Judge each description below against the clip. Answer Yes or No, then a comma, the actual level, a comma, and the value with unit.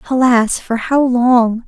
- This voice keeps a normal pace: Yes, average, 145 wpm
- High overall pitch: Yes, high, 245 Hz